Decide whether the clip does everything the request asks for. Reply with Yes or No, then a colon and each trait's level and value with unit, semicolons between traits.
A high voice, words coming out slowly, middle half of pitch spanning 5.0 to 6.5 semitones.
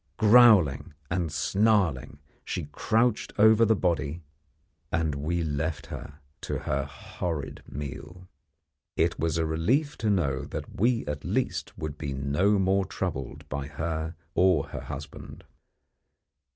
No: very low, 80 Hz; slow, 130 wpm; average, 5.3 semitones